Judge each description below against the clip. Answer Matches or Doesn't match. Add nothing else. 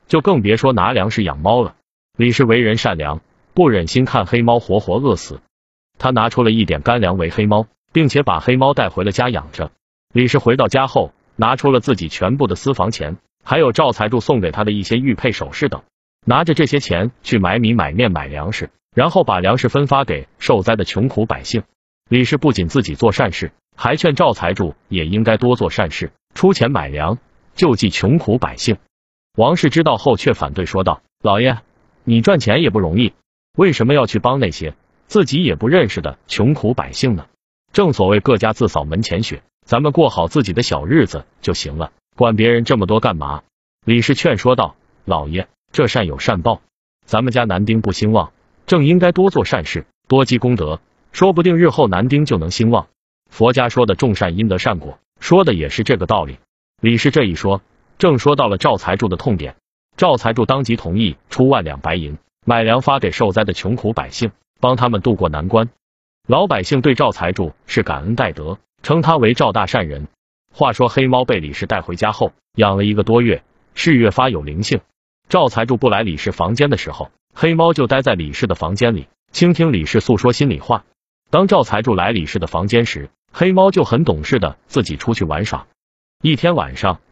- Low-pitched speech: Matches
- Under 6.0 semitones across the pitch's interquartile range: Matches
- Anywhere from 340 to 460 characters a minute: Doesn't match